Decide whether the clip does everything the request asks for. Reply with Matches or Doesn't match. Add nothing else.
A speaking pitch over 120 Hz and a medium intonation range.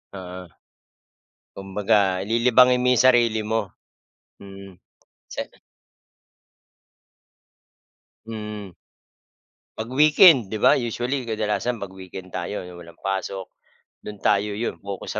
Doesn't match